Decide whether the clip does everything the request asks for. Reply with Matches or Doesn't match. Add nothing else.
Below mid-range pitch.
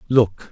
Matches